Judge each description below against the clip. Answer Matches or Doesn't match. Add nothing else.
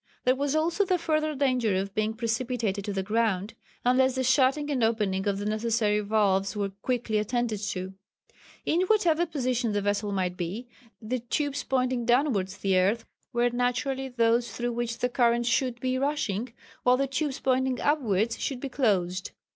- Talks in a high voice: Matches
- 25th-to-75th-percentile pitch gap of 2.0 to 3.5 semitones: Doesn't match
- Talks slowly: Doesn't match